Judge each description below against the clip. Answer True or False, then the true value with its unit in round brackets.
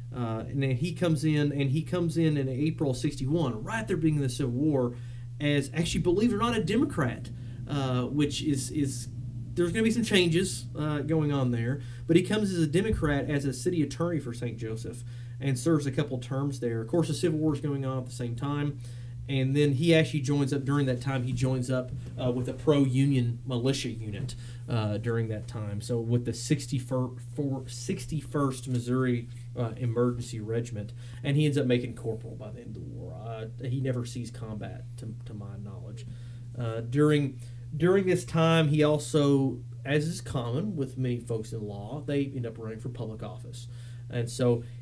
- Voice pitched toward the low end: True (130 Hz)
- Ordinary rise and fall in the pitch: True (3.5 semitones)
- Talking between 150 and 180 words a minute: False (200 wpm)